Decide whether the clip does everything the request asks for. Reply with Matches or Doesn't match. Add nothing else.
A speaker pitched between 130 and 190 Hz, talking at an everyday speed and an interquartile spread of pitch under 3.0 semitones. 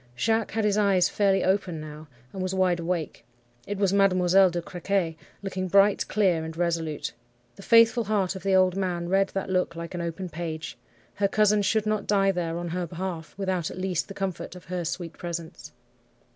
Matches